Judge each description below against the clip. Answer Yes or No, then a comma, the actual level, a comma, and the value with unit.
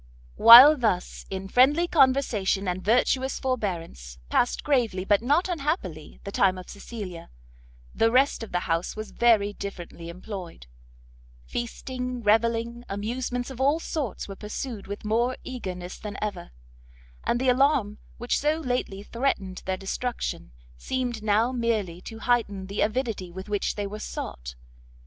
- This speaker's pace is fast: No, average, 145 wpm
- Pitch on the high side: Yes, high, 220 Hz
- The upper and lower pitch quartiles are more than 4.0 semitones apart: Yes, average, 4.5 semitones